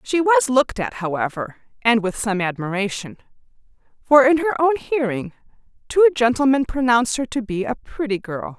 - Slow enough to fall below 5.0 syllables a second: No, 5.2 syllables/s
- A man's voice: No, female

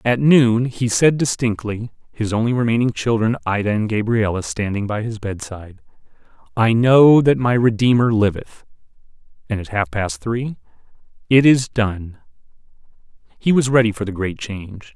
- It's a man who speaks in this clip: Yes, male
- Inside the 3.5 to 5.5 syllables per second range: Yes, 4.8 syllables/s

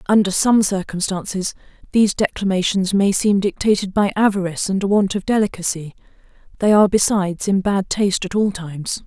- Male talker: No, female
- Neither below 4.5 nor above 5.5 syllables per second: No, 5.7 syllables/s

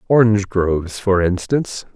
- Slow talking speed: Yes, slow, 90 wpm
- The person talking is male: Yes, male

